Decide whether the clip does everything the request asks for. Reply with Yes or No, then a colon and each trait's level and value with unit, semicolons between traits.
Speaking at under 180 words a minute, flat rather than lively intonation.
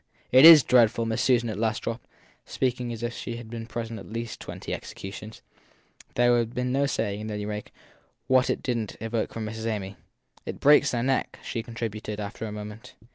No: average, 200 wpm; narrow, 2.1 semitones